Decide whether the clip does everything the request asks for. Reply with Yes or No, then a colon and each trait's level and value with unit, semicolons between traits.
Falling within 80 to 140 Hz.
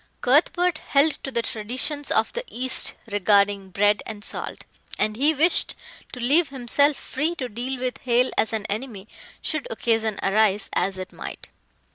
No: high, 240 Hz